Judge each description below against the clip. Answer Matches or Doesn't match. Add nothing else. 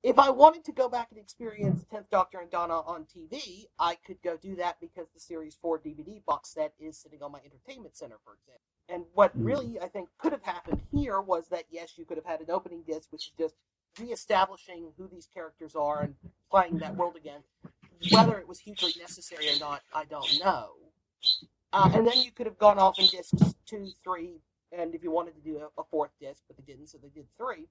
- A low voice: Doesn't match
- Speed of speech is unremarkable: Doesn't match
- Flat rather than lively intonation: Doesn't match